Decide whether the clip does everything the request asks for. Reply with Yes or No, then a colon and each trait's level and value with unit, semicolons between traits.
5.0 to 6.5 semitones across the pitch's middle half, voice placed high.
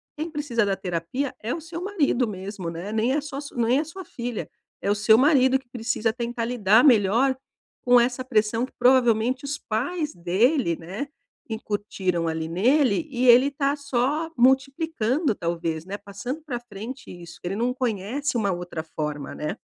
Yes: wide, 5.4 semitones; high, 240 Hz